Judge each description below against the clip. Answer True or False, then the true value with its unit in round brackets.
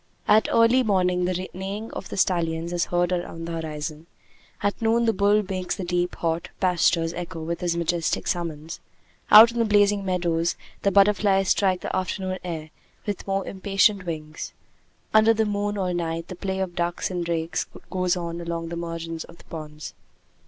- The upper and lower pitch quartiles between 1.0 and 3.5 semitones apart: True (2.9 semitones)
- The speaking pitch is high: False (180 Hz)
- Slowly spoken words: False (180 wpm)